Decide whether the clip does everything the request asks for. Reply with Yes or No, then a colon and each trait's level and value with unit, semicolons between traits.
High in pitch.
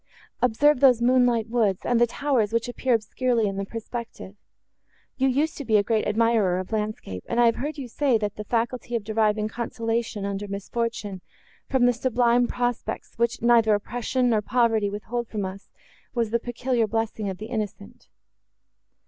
Yes: high, 230 Hz